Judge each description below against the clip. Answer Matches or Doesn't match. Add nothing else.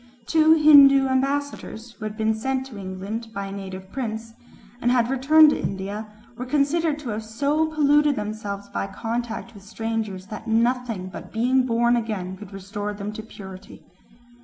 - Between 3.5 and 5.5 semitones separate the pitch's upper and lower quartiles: Matches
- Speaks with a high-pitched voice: Matches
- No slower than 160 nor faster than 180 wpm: Matches